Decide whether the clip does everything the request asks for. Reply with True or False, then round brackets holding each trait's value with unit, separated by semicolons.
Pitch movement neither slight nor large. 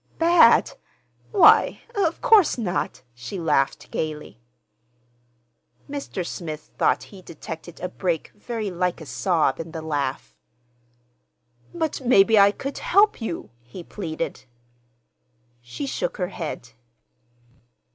False (8.2 semitones)